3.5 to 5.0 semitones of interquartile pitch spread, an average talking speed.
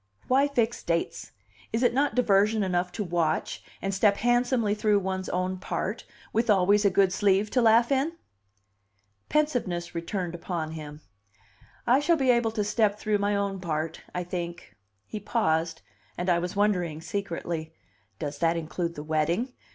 Yes: average, 4.6 semitones; average, 160 wpm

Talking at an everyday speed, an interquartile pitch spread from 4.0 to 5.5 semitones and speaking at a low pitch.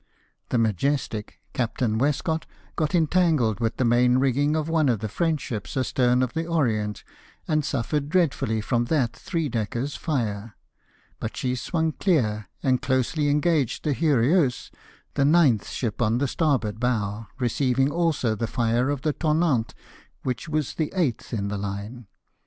Yes: average, 155 wpm; average, 5.0 semitones; low, 130 Hz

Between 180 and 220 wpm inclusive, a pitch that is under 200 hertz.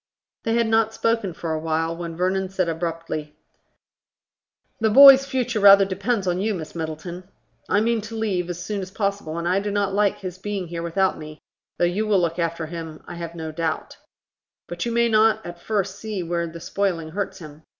Yes: average, 200 wpm; medium, 185 Hz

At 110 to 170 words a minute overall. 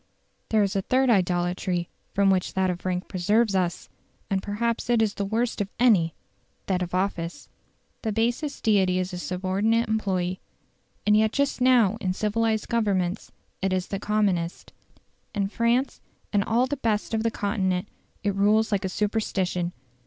Yes: average, 165 wpm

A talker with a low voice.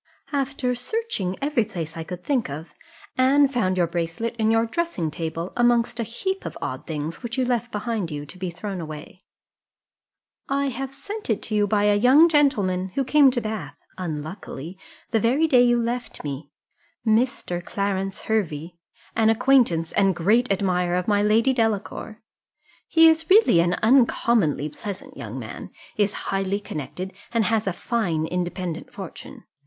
No: high, 210 Hz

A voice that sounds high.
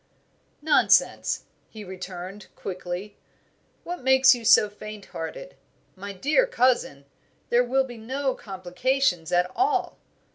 Yes: high, 220 Hz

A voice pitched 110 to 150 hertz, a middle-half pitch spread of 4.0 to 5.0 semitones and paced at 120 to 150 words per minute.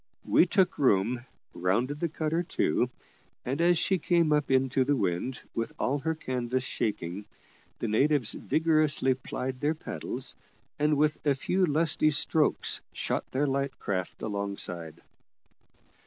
Yes: low, 135 Hz; average, 4.3 semitones; average, 140 wpm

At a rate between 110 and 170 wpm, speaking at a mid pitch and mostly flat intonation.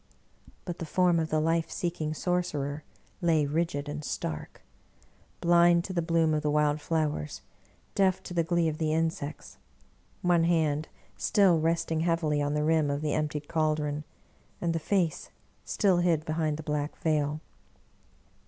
Yes: average, 160 wpm; medium, 160 Hz; narrow, 2.2 semitones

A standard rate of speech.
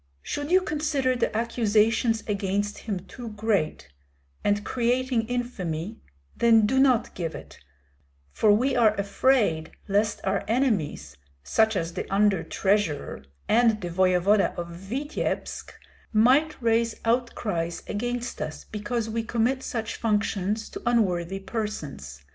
No: slow, 125 wpm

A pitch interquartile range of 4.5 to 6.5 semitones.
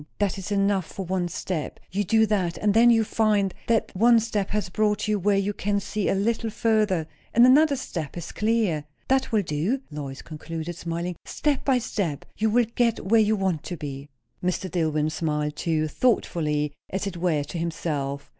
Yes: average, 4.9 semitones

